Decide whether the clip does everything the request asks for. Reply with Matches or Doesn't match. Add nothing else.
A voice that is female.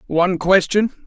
Doesn't match